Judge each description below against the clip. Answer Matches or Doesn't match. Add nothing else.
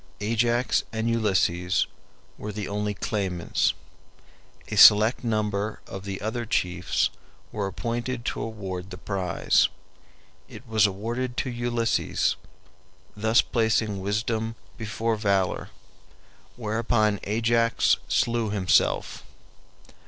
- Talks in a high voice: Doesn't match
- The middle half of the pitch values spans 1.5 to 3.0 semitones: Matches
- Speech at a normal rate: Doesn't match